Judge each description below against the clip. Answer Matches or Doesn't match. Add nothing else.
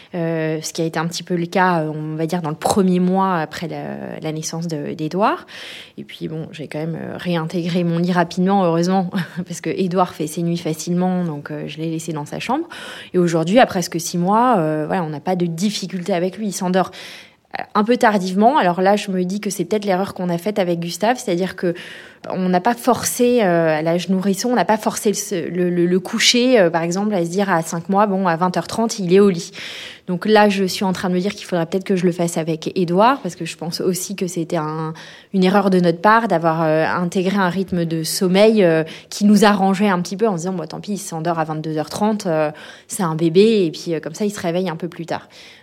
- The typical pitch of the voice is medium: Matches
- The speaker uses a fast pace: Matches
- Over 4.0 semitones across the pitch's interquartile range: Doesn't match